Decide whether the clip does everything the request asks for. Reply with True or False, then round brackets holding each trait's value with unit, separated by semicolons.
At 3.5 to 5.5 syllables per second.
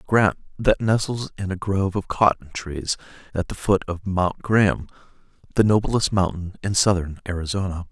True (4.9 syllables/s)